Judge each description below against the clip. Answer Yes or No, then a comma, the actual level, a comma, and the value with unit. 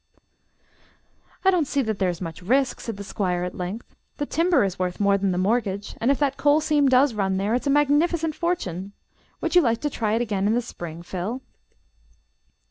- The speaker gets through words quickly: Yes, fast, 210 wpm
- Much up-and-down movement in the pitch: Yes, wide, 7.0 semitones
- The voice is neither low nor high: No, high, 225 Hz